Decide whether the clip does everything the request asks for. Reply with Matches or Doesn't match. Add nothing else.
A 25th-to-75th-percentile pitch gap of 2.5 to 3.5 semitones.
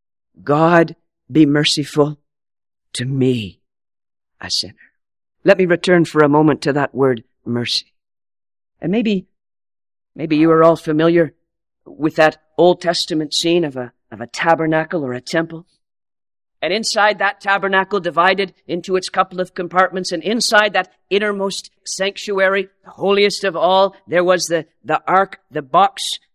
Doesn't match